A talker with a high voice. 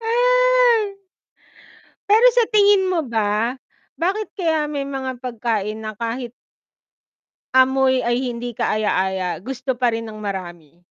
Yes: very high, 255 Hz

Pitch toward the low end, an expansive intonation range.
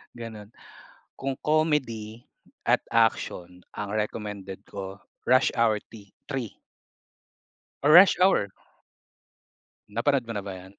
No: low, 115 Hz; average, 4.6 semitones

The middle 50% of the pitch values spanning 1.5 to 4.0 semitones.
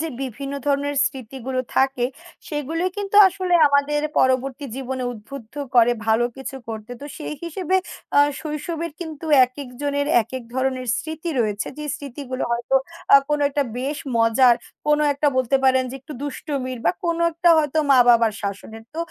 Yes: average, 3.0 semitones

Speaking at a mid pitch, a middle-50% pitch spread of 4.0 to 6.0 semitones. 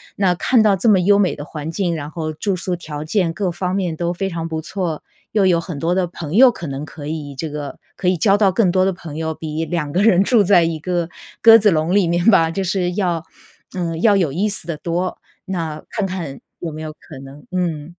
No: medium, 175 Hz; average, 3.3 semitones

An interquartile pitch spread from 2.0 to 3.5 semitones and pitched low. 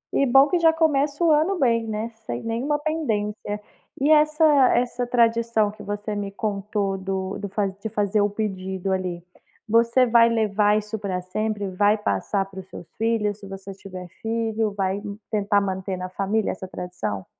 No: average, 3.1 semitones; high, 210 Hz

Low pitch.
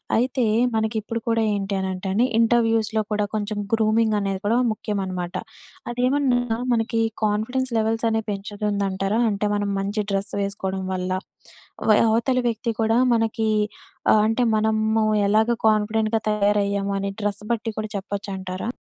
No: high, 215 Hz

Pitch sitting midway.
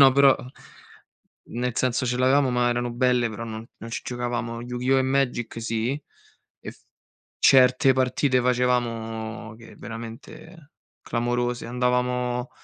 No: low, 125 Hz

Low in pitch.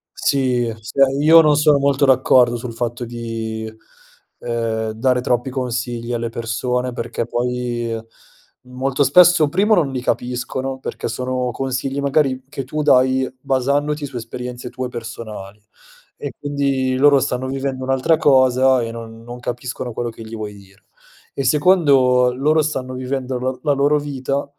Yes: low, 130 Hz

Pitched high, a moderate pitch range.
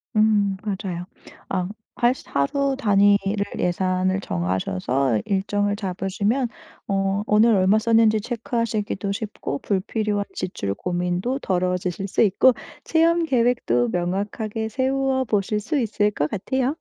Yes: high, 205 Hz; average, 3.8 semitones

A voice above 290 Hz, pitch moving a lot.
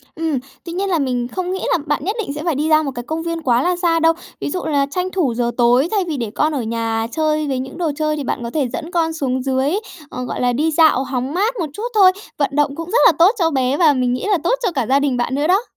No: very high, 300 Hz; average, 4.5 semitones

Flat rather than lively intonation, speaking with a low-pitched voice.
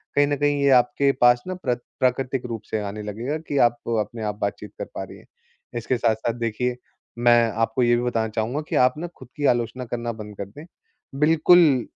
No: average, 3.6 semitones; low, 120 Hz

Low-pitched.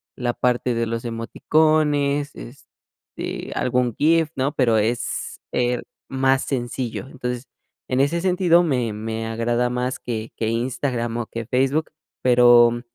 Yes: low, 125 Hz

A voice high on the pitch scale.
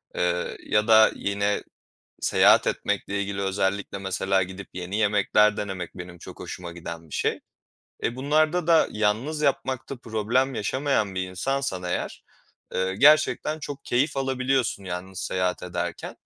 No: low, 100 Hz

